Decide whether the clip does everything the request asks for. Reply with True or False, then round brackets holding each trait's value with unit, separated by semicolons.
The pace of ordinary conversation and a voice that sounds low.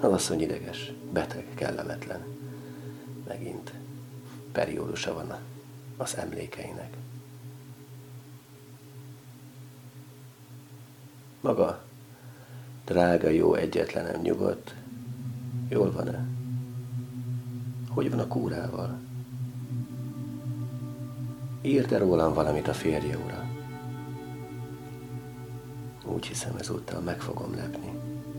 False (70 wpm; 125 Hz)